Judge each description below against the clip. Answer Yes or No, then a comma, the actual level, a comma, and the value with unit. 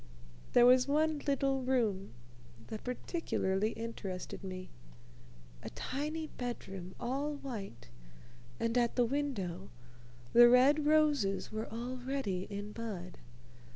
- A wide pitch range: Yes, wide, 5.7 semitones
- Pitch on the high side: Yes, high, 240 Hz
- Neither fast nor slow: No, slow, 110 wpm